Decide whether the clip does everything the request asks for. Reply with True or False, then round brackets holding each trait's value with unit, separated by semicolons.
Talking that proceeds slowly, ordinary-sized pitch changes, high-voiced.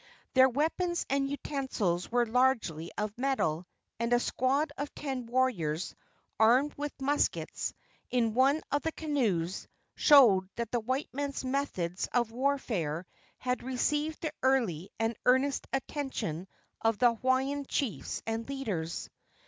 True (130 wpm; 4.2 semitones; 255 Hz)